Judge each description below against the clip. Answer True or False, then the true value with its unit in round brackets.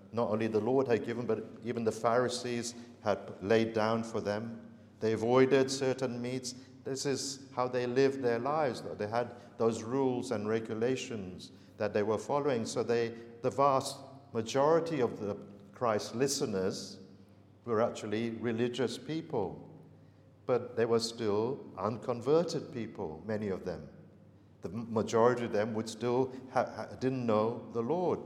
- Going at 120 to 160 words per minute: True (150 wpm)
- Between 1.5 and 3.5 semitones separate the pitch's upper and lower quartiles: True (2.8 semitones)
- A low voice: True (120 Hz)